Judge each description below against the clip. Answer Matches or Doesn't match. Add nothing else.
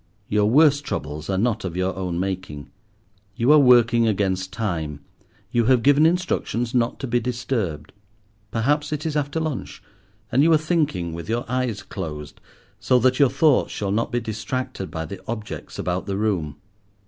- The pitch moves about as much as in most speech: Doesn't match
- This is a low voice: Matches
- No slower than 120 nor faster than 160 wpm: Doesn't match